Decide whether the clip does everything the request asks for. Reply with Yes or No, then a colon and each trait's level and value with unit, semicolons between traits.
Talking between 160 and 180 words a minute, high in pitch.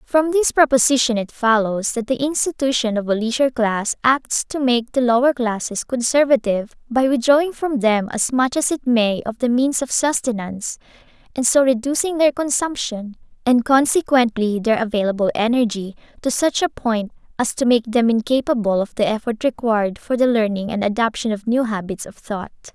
Yes: average, 175 wpm; high, 240 Hz